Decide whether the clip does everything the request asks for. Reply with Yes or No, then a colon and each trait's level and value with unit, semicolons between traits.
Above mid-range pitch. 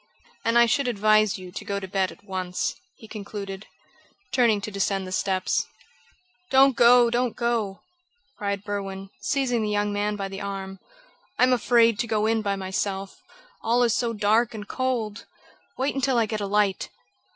Yes: high, 210 Hz